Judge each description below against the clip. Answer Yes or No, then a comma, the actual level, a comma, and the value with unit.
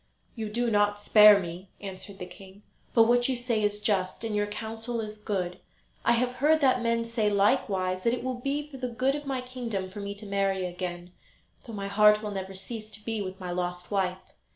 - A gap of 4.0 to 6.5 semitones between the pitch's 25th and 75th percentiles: No, average, 3.5 semitones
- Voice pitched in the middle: No, high, 210 Hz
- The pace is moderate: No, fast, 220 wpm